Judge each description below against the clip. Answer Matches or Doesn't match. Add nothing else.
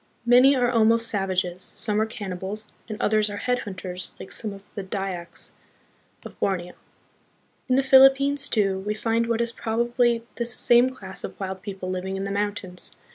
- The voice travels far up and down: Doesn't match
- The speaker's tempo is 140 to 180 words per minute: Matches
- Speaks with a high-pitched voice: Matches